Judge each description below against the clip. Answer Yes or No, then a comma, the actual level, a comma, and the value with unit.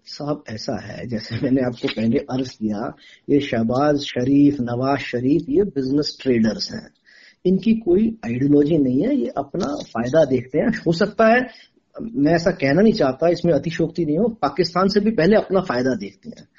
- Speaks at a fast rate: No, average, 175 wpm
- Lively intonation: Yes, wide, 6.8 semitones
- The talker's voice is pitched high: No, medium, 145 Hz